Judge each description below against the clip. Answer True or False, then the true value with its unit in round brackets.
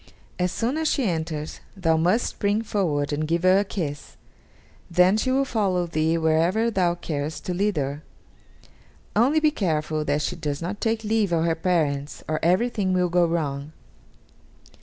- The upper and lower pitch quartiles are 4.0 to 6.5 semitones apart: True (4.8 semitones)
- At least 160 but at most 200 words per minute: True (170 wpm)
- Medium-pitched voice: True (175 Hz)